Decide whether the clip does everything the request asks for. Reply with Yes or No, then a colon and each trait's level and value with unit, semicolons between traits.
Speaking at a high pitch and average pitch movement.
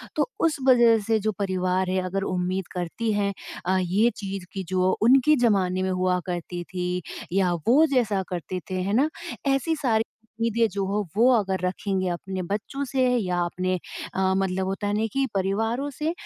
Yes: high, 195 Hz; average, 3.7 semitones